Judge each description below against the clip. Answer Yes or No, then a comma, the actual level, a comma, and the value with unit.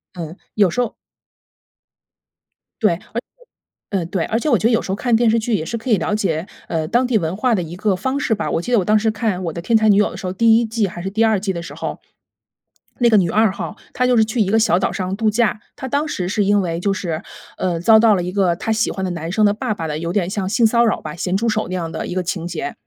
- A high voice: Yes, high, 205 Hz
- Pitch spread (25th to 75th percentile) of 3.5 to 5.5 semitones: Yes, average, 3.9 semitones